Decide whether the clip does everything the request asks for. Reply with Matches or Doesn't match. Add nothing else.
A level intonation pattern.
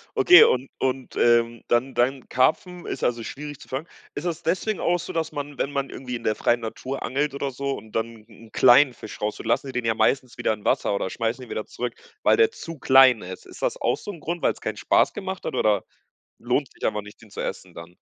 Doesn't match